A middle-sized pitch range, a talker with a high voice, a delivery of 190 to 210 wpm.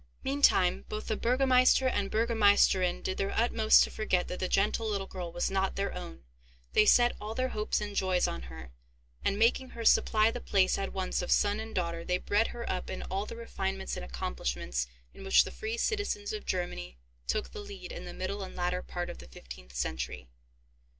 Yes: average, 3.7 semitones; high, 195 Hz; fast, 205 wpm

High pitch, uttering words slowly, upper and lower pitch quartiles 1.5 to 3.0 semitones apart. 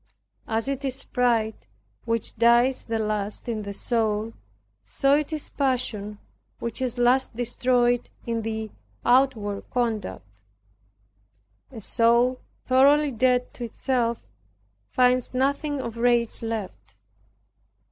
Yes: high, 240 Hz; slow, 115 wpm; narrow, 2.6 semitones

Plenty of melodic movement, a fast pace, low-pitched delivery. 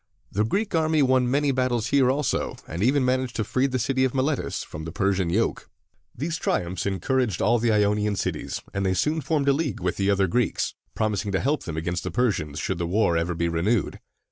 Yes: wide, 5.9 semitones; fast, 215 wpm; low, 110 Hz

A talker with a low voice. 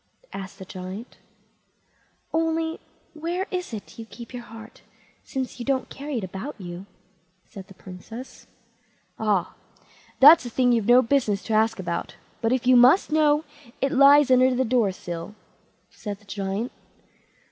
No: high, 240 Hz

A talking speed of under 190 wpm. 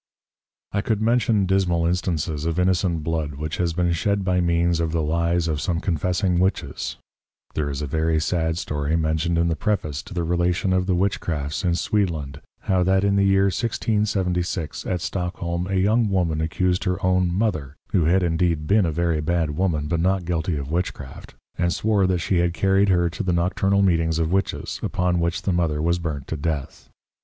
No: average, 195 wpm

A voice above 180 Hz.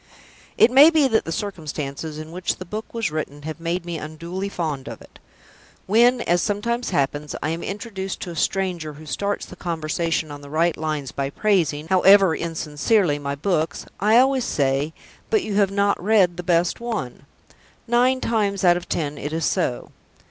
No: medium, 175 Hz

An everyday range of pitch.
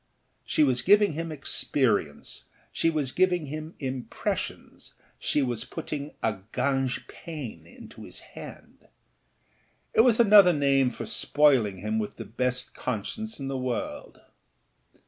Yes: average, 4.4 semitones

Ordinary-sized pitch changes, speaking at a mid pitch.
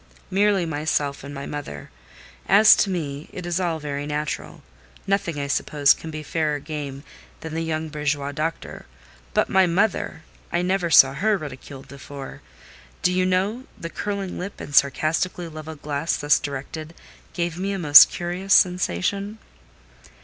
Yes: average, 4.1 semitones; medium, 160 Hz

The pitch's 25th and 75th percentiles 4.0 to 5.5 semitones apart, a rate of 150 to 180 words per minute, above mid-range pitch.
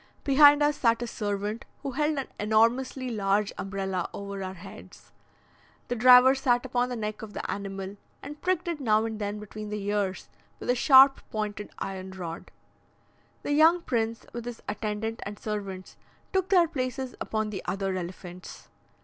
Yes: average, 4.6 semitones; average, 165 wpm; high, 220 Hz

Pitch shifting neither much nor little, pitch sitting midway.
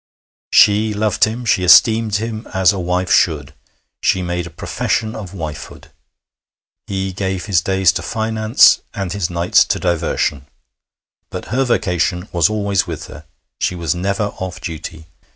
No: average, 3.5 semitones; very low, 95 Hz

